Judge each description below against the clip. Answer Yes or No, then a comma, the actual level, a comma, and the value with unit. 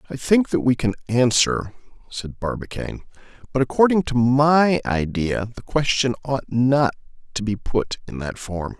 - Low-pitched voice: Yes, low, 125 Hz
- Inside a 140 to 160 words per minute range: Yes, average, 155 wpm